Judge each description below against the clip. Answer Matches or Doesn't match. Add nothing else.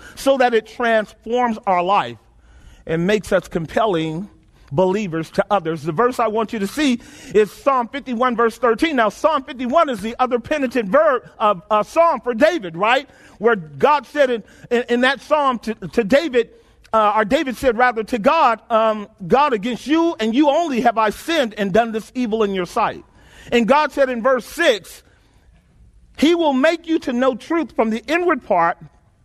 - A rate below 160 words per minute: Doesn't match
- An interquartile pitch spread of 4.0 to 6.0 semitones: Matches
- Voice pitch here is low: Doesn't match